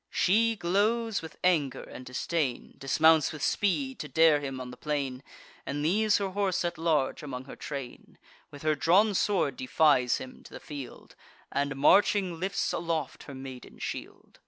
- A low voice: No, medium, 155 Hz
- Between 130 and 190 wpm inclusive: Yes, average, 165 wpm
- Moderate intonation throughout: No, wide, 5.7 semitones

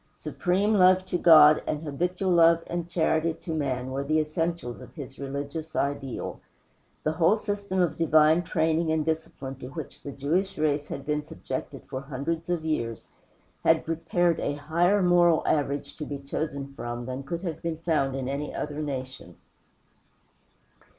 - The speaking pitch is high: No, medium, 155 Hz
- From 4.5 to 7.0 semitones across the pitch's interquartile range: No, average, 3.3 semitones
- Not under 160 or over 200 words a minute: Yes, average, 165 wpm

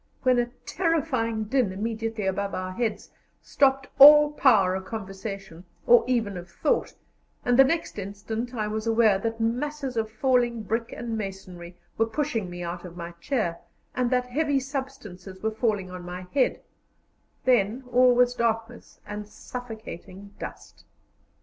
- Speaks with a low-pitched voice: No, high, 225 Hz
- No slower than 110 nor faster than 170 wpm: Yes, average, 150 wpm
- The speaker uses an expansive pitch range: No, average, 4.3 semitones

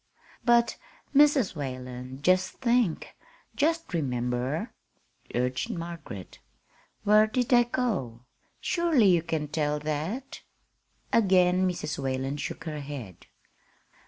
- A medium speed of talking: No, slow, 100 wpm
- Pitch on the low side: No, medium, 165 Hz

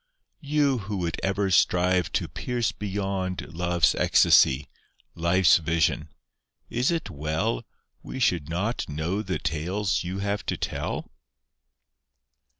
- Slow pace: Yes, slow, 120 wpm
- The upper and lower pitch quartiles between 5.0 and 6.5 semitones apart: No, average, 3.7 semitones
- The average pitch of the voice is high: No, very low, 95 Hz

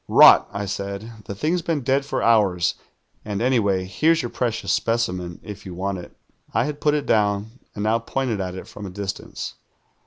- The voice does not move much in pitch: No, average, 4.5 semitones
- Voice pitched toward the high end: No, low, 105 Hz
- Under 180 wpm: No, average, 190 wpm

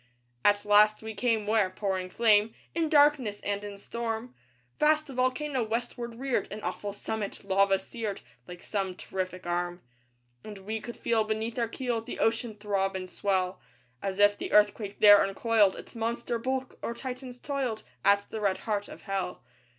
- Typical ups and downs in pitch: Yes, average, 3.0 semitones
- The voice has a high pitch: Yes, high, 215 Hz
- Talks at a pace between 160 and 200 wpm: Yes, average, 170 wpm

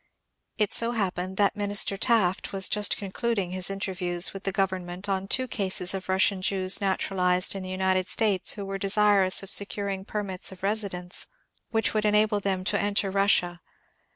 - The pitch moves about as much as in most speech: No, narrow, 1.7 semitones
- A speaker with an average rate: Yes, average, 180 wpm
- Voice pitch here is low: No, high, 195 Hz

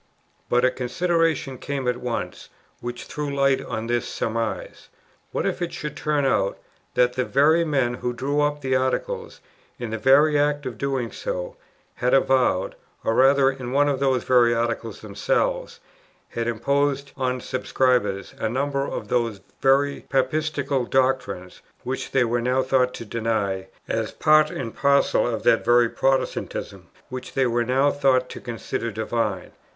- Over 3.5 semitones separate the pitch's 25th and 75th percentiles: No, average, 2.9 semitones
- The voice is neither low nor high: No, low, 130 Hz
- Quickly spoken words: No, average, 160 wpm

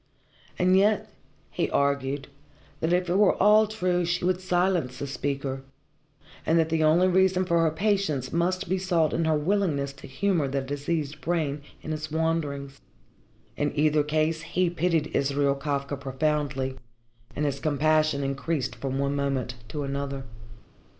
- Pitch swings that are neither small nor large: Yes, average, 4.0 semitones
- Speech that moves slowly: No, average, 155 wpm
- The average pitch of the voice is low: No, medium, 155 Hz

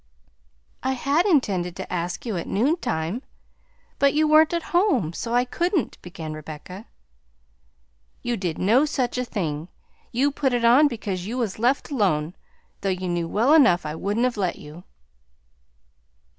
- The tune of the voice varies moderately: No, wide, 7.3 semitones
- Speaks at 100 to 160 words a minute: Yes, average, 155 wpm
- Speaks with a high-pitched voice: Yes, high, 225 Hz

